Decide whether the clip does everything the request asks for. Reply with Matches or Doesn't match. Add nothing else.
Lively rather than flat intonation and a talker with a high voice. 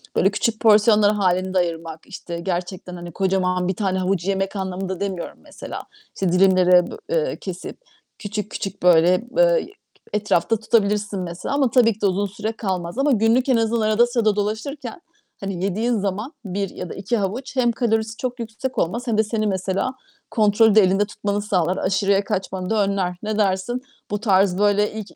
Doesn't match